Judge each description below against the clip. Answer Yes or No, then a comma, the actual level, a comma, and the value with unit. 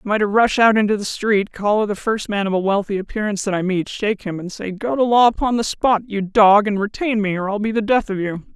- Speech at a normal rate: No, fast, 290 wpm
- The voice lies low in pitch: No, high, 210 Hz